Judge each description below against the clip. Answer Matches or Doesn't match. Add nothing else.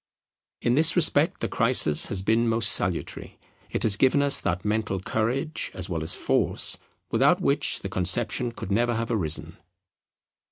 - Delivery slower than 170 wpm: Matches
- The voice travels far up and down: Doesn't match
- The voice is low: Matches